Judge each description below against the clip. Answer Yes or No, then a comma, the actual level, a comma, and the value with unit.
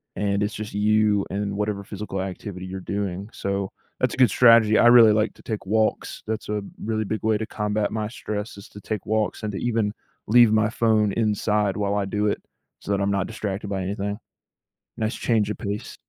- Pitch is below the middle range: Yes, low, 105 Hz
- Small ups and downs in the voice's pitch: Yes, narrow, 1.5 semitones